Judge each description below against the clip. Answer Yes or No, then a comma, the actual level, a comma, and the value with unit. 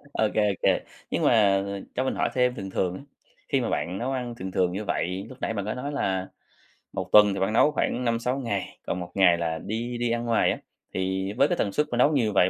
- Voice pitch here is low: Yes, low, 105 Hz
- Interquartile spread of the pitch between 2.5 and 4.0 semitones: No, average, 4.6 semitones